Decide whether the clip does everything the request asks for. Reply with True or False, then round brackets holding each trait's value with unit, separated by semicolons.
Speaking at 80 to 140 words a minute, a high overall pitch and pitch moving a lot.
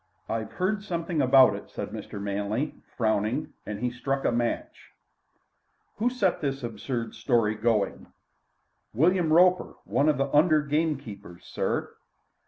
False (135 wpm; 135 Hz; 6.0 semitones)